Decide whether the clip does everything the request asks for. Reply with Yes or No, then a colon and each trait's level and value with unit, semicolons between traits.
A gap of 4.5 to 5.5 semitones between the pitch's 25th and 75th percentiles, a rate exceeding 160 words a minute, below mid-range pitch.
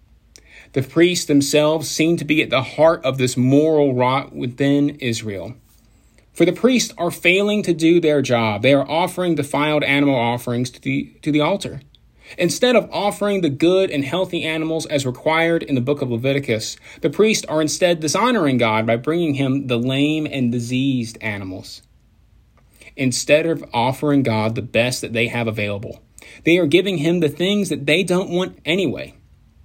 No: average, 5.0 semitones; average, 170 wpm; medium, 145 Hz